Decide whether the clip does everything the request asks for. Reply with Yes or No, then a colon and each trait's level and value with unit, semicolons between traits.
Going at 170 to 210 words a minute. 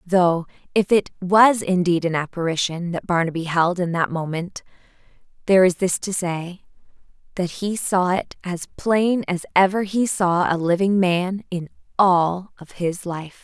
No: average, 160 wpm